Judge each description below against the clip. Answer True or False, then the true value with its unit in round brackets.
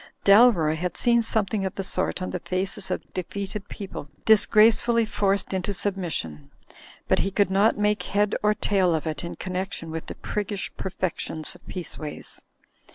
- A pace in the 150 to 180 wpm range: True (165 wpm)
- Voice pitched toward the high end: True (195 Hz)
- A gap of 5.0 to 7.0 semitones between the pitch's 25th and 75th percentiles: False (2.6 semitones)